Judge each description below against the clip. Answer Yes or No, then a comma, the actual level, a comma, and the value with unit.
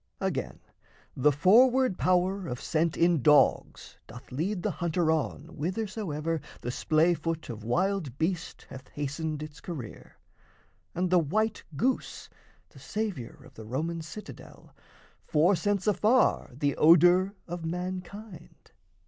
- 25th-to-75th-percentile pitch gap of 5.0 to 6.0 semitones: No, average, 4.1 semitones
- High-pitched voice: No, medium, 170 Hz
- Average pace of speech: No, slow, 125 wpm